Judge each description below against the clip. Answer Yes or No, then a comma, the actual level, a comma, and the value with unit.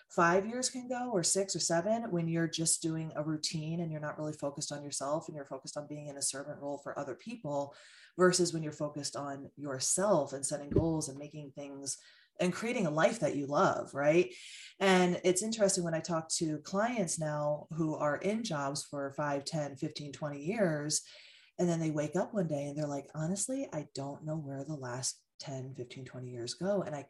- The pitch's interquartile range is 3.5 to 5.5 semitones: Yes, average, 4.0 semitones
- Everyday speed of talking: No, fast, 215 wpm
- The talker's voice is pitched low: No, medium, 155 Hz